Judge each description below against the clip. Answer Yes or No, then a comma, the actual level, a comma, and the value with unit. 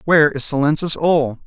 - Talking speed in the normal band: Yes, average, 165 wpm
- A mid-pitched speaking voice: Yes, medium, 150 Hz